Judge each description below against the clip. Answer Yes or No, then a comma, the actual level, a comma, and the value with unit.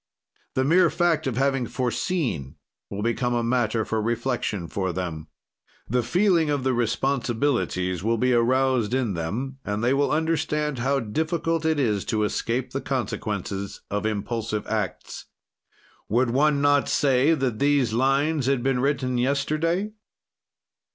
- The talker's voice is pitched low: Yes, low, 125 Hz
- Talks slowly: No, average, 145 wpm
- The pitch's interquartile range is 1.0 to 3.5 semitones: No, average, 4.4 semitones